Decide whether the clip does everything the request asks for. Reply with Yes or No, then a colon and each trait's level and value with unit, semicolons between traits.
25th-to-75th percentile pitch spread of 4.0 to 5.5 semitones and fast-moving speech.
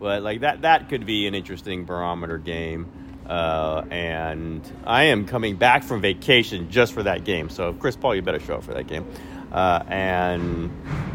No: average, 4.3 semitones; average, 185 wpm